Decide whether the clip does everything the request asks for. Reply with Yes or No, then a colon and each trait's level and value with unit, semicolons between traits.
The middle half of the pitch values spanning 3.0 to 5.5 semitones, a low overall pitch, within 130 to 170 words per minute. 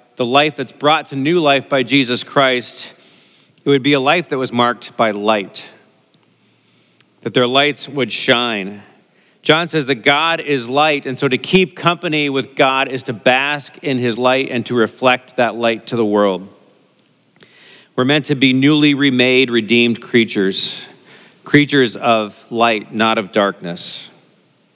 Yes: average, 3.5 semitones; low, 130 Hz; average, 160 wpm